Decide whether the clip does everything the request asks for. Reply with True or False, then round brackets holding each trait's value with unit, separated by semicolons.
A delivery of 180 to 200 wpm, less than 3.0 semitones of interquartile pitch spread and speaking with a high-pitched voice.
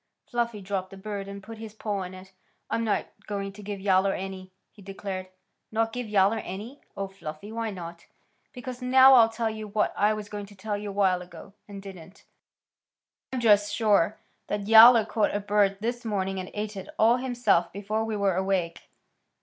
True (190 wpm; 2.4 semitones; 205 Hz)